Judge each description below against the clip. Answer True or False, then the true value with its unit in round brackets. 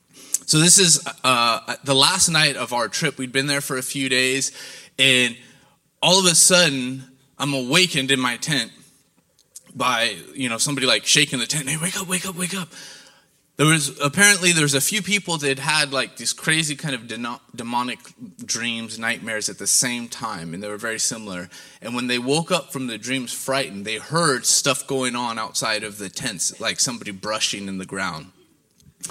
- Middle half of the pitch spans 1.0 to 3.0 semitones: False (4.5 semitones)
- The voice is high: False (135 Hz)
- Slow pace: False (195 wpm)